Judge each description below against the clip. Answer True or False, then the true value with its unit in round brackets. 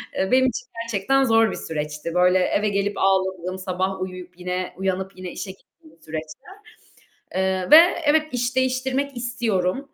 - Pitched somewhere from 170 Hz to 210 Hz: True (190 Hz)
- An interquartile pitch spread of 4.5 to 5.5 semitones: True (4.8 semitones)